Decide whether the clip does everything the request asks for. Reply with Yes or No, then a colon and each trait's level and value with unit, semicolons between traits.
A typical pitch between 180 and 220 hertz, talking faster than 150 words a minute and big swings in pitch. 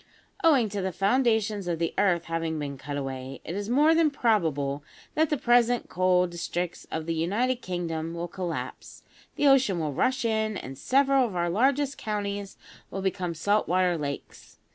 Yes: high, 190 Hz; average, 175 wpm; wide, 6.3 semitones